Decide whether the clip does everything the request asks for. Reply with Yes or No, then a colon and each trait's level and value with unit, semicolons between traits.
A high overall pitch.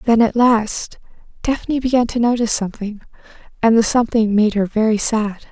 Yes: high, 225 Hz